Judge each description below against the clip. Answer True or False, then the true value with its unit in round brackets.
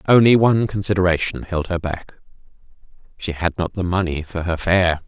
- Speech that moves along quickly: False (155 wpm)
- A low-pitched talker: True (90 Hz)